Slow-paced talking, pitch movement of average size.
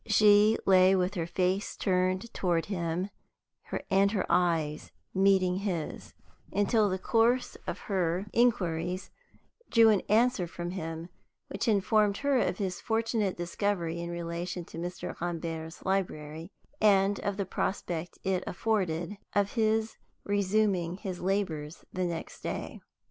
Yes: slow, 130 wpm; average, 3.0 semitones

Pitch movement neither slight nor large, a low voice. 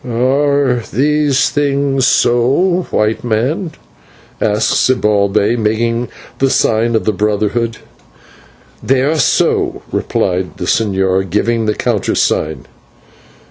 Yes: average, 4.3 semitones; low, 120 Hz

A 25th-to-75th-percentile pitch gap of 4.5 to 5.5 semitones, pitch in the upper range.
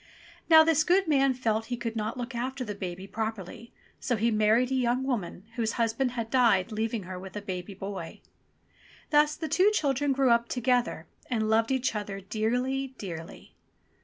No: average, 3.9 semitones; high, 235 Hz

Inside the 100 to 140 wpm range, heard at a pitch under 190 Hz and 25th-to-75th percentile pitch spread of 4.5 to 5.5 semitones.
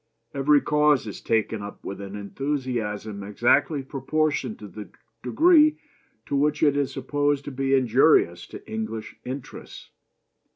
Yes: slow, 135 wpm; low, 135 Hz; average, 5.0 semitones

